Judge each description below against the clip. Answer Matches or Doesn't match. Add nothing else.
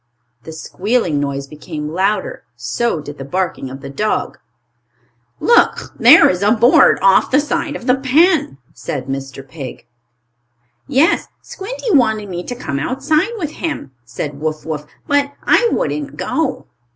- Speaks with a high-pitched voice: Matches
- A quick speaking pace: Doesn't match